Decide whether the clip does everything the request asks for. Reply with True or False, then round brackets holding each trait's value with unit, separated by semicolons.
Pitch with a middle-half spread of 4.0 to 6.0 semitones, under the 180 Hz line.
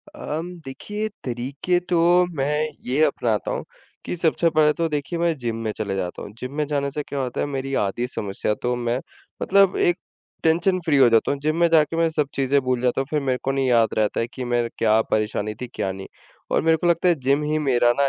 True (4.8 semitones; 135 Hz)